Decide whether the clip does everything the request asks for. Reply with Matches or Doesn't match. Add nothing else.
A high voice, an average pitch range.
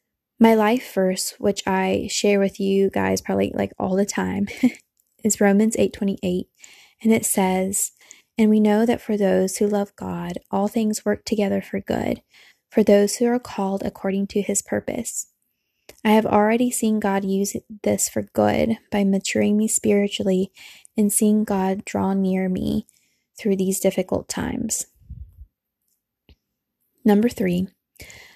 Doesn't match